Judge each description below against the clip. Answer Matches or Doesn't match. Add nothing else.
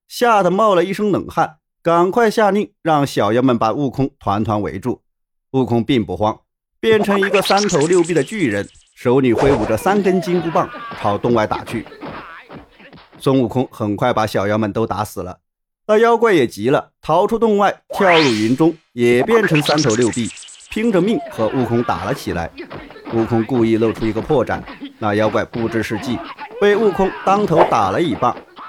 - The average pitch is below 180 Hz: Matches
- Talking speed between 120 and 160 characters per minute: Doesn't match